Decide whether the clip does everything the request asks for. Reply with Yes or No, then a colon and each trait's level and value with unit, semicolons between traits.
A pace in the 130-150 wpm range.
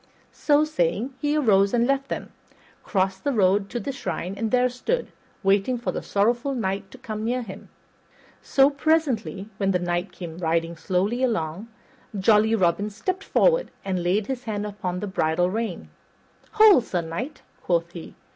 No: average, 165 wpm